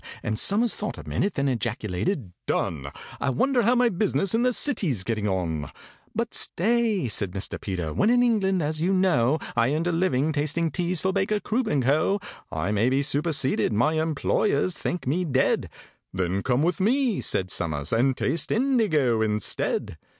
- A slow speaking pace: No, average, 170 wpm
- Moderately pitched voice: Yes, medium, 155 Hz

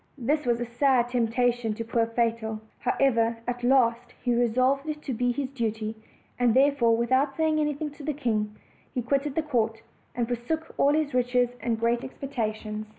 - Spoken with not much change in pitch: No, average, 3.1 semitones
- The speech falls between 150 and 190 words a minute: Yes, average, 175 wpm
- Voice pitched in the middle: No, high, 245 Hz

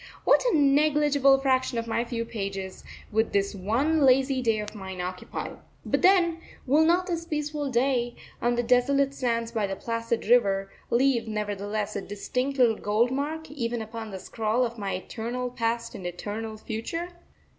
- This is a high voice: Yes, high, 235 Hz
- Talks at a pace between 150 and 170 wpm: Yes, average, 165 wpm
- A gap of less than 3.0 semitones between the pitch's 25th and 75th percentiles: No, average, 4.3 semitones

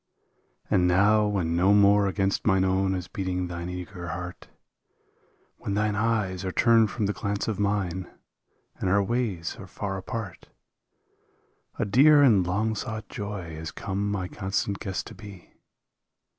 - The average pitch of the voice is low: Yes, low, 100 Hz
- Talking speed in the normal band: Yes, average, 155 wpm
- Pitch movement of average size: No, narrow, 2.2 semitones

